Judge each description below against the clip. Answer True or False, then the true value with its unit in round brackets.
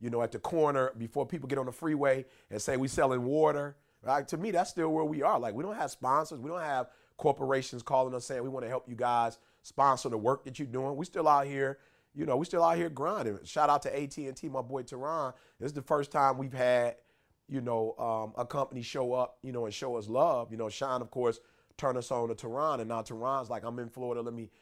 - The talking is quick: True (260 wpm)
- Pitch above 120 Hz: True (135 Hz)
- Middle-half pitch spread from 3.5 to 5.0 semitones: False (3.0 semitones)